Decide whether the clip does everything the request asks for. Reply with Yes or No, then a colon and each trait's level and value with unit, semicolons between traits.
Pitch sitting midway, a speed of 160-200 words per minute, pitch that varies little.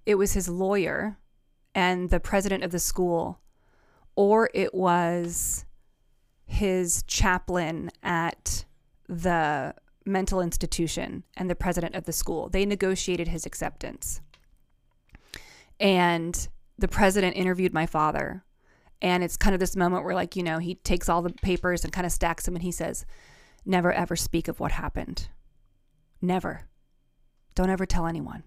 No: medium, 180 Hz; average, 145 wpm; narrow, 1.9 semitones